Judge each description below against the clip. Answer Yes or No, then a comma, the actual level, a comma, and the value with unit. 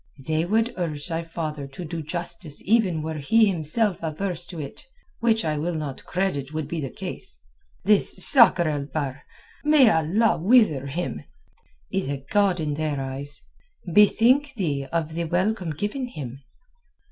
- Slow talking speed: No, average, 150 wpm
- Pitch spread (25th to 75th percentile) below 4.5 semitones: No, average, 5.2 semitones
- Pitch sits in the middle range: Yes, medium, 165 Hz